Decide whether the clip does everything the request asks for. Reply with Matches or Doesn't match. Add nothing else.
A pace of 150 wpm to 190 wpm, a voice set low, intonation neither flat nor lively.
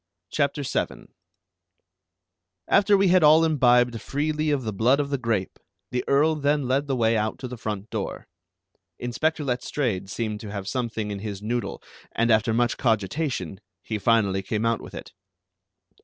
Matches